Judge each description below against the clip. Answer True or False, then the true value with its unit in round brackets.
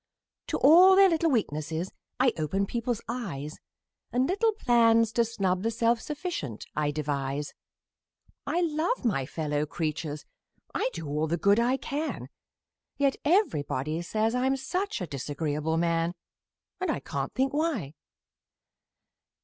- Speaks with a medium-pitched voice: False (215 Hz)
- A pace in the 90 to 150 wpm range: True (135 wpm)